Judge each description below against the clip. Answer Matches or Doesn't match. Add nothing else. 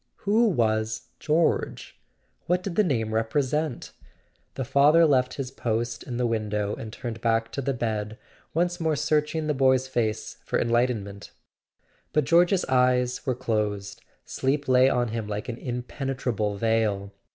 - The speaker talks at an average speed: Matches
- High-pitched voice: Doesn't match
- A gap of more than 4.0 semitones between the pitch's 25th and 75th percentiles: Matches